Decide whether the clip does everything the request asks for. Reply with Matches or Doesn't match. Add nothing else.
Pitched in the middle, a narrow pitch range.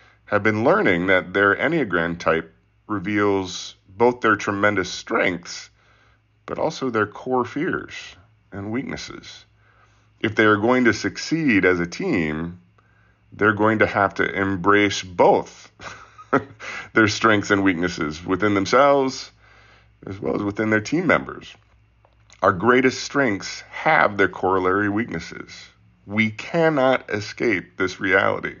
Doesn't match